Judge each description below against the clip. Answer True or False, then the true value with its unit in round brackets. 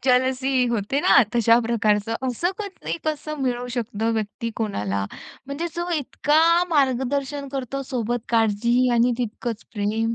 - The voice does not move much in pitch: False (3.5 semitones)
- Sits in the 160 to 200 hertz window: False (245 Hz)